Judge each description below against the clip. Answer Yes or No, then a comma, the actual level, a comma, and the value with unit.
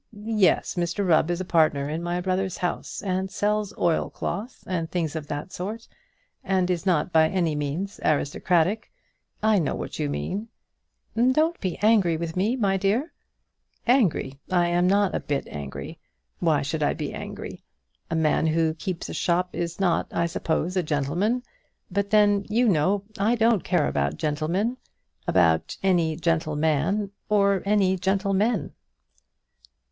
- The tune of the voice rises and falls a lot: No, average, 4.1 semitones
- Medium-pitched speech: Yes, medium, 180 Hz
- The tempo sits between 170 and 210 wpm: No, average, 150 wpm